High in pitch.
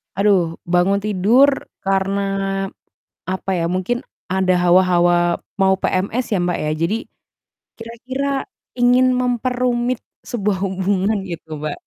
Yes: high, 195 Hz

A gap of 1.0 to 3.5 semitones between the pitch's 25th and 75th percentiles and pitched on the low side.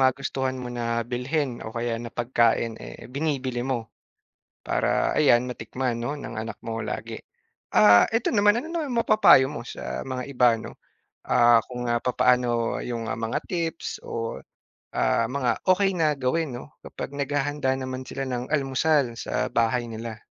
Yes: average, 3.2 semitones; low, 125 Hz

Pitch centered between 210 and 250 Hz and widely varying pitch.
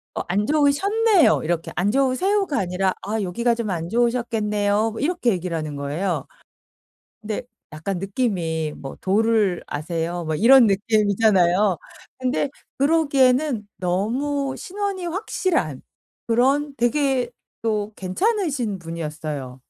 Yes: high, 215 Hz; wide, 7.3 semitones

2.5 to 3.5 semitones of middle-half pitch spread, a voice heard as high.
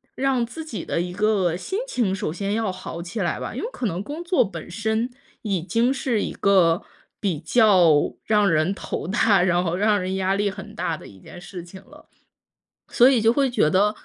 No: average, 4.3 semitones; high, 200 Hz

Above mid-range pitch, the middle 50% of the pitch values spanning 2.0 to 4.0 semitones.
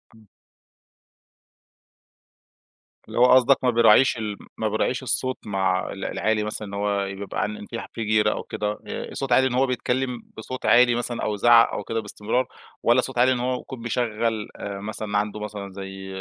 No: low, 110 Hz; average, 3.1 semitones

